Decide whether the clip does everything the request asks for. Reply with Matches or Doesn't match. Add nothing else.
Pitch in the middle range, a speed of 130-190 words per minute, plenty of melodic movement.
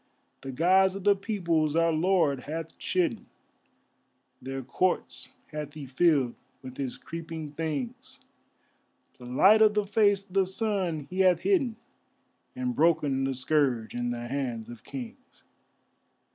Matches